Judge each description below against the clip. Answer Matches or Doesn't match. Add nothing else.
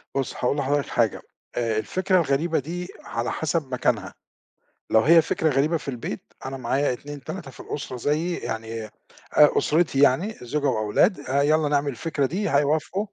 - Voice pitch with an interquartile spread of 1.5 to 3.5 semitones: Doesn't match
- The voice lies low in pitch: Doesn't match